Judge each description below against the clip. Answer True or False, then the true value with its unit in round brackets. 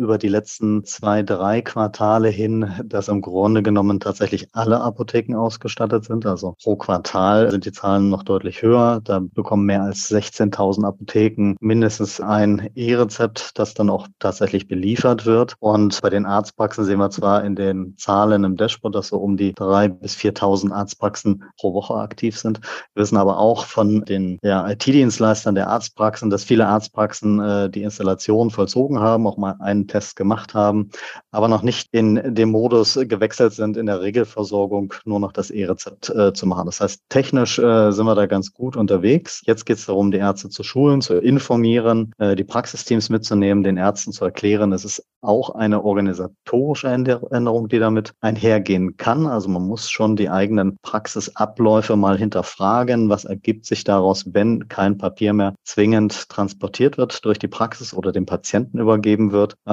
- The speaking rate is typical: True (175 wpm)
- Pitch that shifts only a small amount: True (2.1 semitones)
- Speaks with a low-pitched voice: True (105 Hz)